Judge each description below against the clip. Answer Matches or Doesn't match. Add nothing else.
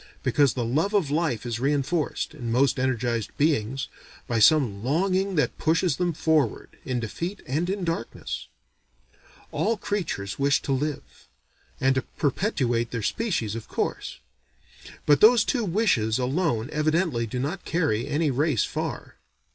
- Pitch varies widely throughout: Matches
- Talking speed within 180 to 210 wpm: Doesn't match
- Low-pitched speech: Doesn't match